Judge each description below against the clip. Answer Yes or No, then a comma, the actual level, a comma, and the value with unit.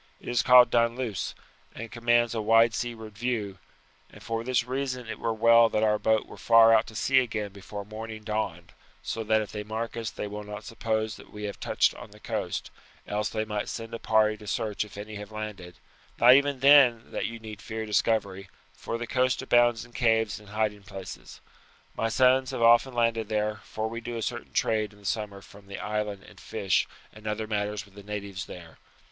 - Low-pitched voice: Yes, low, 110 Hz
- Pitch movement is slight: Yes, narrow, 1.9 semitones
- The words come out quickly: Yes, fast, 210 wpm